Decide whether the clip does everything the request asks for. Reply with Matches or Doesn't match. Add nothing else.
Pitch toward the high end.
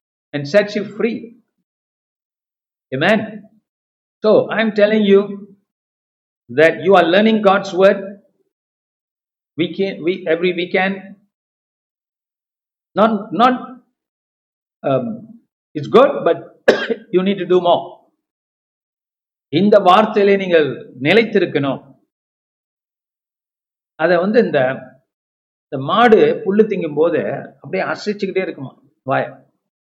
Matches